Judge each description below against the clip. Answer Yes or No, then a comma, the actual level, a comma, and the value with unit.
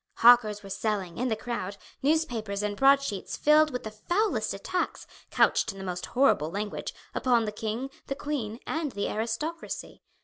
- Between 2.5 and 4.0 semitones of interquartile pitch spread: No, average, 4.9 semitones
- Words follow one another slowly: No, average, 165 wpm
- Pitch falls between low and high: No, high, 225 Hz